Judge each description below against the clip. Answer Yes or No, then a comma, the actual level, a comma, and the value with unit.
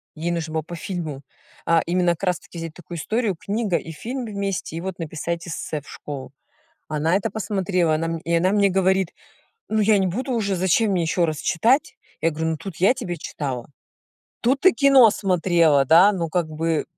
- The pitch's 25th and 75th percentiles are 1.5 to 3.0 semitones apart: No, average, 3.6 semitones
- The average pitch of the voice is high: No, medium, 175 Hz